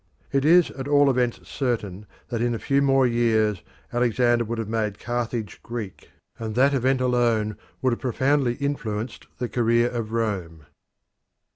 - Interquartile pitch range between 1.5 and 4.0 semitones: Yes, average, 2.8 semitones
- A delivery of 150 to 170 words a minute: Yes, average, 155 wpm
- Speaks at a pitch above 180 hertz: No, low, 120 Hz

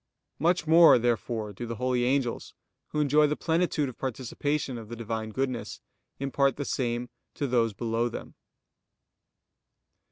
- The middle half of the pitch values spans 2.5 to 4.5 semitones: Yes, average, 3.5 semitones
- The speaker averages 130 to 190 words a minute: Yes, average, 140 wpm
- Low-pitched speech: Yes, low, 125 Hz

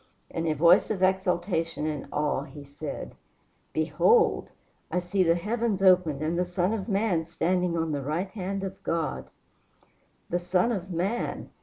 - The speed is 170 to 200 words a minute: No, average, 160 wpm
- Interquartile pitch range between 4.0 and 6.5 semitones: No, average, 2.9 semitones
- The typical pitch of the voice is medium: Yes, medium, 175 Hz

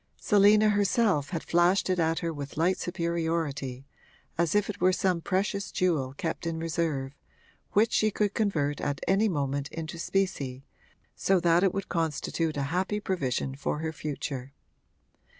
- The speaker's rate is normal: Yes, average, 155 wpm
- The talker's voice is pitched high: No, medium, 170 Hz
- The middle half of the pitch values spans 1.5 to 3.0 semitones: No, average, 4.8 semitones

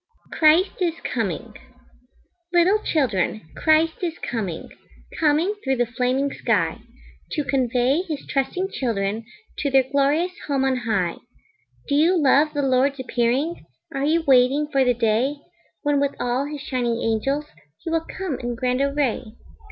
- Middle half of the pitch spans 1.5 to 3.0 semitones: No, average, 3.7 semitones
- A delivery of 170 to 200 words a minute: No, average, 145 wpm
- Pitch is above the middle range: Yes, very high, 275 Hz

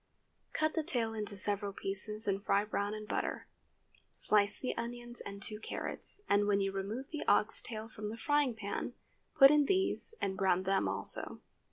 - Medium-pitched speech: No, high, 215 Hz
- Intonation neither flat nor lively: Yes, average, 3.2 semitones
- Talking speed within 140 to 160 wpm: No, average, 180 wpm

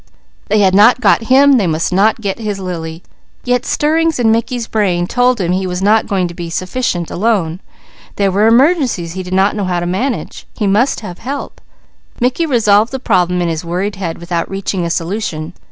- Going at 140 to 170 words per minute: No, average, 200 wpm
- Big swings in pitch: No, average, 4.7 semitones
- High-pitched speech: Yes, high, 200 Hz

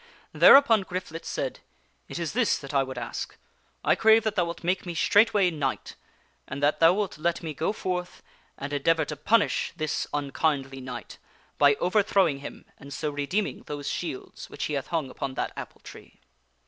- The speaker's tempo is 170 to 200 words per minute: Yes, average, 185 wpm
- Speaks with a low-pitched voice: No, medium, 160 Hz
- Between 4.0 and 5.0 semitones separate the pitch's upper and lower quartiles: Yes, average, 4.7 semitones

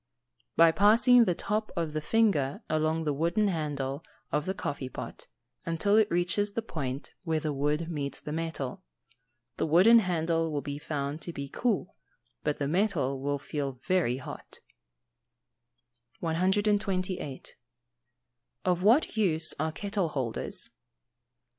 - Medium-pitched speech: Yes, medium, 165 Hz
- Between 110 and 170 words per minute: Yes, average, 140 wpm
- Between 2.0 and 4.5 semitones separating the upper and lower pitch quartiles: No, average, 5.1 semitones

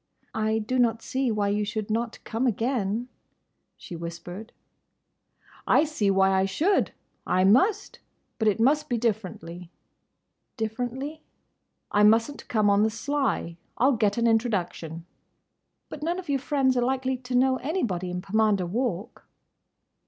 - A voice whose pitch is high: Yes, high, 225 Hz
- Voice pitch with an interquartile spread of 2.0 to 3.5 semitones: No, average, 4.5 semitones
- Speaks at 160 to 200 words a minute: No, average, 140 wpm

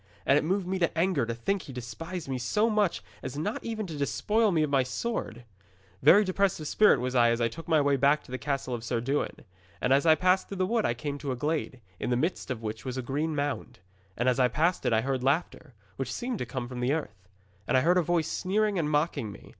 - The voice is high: No, medium, 145 Hz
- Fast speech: Yes, fast, 260 wpm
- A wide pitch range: Yes, wide, 6.1 semitones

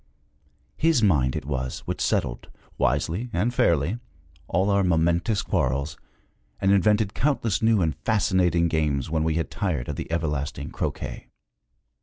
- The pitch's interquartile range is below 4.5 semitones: No, wide, 5.5 semitones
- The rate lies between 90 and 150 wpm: Yes, average, 140 wpm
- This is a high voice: No, very low, 85 Hz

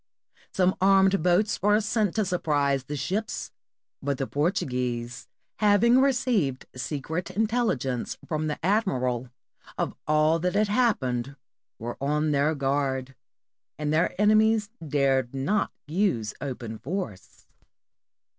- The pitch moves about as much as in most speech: No, wide, 7.4 semitones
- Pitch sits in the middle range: Yes, medium, 155 Hz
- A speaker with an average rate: No, slow, 115 wpm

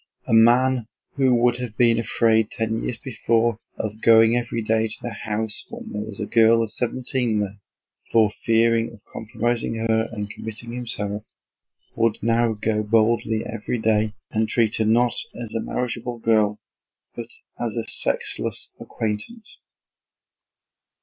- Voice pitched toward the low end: Yes, low, 115 Hz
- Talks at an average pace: Yes, average, 150 wpm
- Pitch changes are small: Yes, narrow, 1.4 semitones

